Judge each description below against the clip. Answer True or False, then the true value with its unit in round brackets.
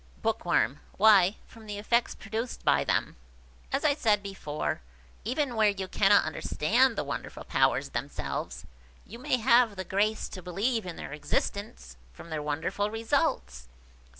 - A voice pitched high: True (205 Hz)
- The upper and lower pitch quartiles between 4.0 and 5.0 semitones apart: True (4.3 semitones)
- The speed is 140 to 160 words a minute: True (150 wpm)